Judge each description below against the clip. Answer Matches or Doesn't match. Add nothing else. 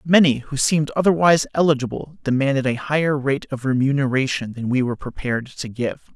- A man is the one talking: Matches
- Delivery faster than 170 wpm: Doesn't match